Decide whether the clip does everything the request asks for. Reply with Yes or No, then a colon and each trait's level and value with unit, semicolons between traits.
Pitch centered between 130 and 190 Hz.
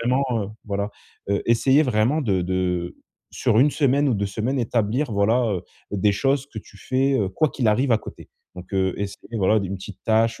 No: low, 110 Hz